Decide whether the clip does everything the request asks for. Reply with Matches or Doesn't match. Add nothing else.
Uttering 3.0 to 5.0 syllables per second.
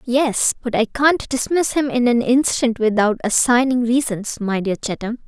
Matches